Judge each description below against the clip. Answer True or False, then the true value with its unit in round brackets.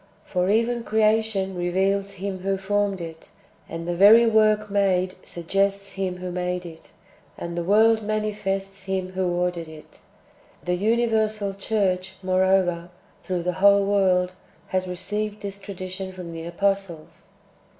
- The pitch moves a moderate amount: False (2.2 semitones)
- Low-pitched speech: False (195 Hz)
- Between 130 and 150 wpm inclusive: True (140 wpm)